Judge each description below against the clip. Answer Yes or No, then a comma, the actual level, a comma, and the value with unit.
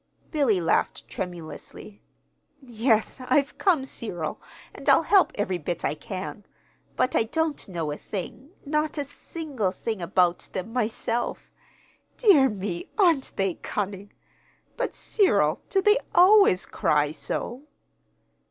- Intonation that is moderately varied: No, wide, 8.0 semitones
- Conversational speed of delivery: No, slow, 125 wpm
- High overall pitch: Yes, high, 225 Hz